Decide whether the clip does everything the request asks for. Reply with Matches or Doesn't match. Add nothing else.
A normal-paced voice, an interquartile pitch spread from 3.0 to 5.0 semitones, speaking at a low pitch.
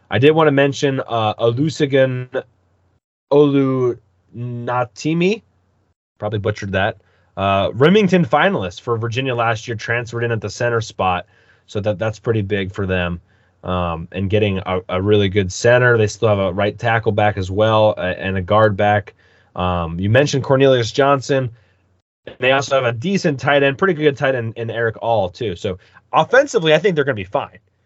Doesn't match